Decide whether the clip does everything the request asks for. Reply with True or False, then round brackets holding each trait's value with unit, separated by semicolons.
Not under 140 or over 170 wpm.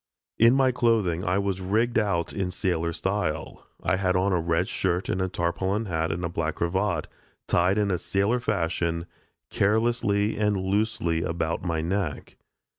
True (155 wpm)